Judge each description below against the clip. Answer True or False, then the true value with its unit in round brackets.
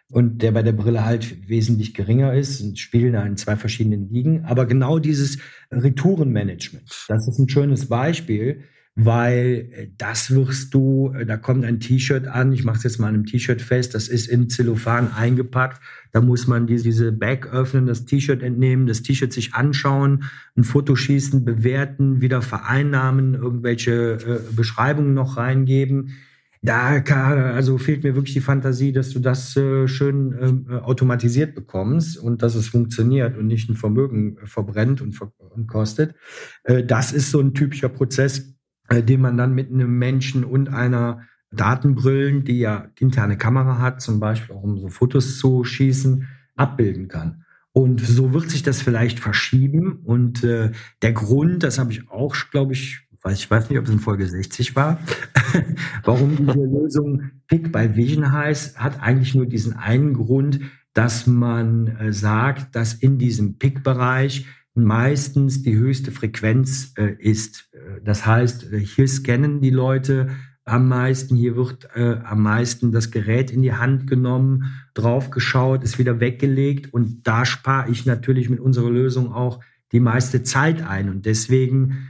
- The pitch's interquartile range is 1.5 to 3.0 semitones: True (2.6 semitones)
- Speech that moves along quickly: False (160 wpm)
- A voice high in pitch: False (125 Hz)